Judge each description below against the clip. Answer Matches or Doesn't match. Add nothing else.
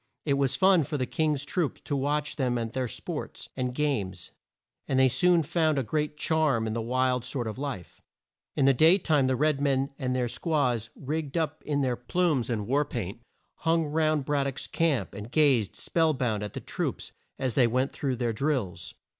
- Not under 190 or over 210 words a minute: Matches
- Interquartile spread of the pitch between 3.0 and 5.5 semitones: Matches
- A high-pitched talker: Doesn't match